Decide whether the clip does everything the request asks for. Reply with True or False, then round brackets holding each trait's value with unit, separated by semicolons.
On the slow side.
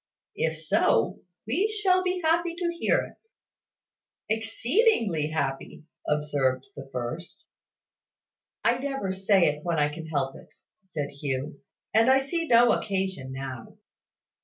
True (130 wpm)